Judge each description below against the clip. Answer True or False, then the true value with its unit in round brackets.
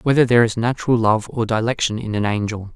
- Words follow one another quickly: True (215 wpm)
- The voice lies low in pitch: True (115 Hz)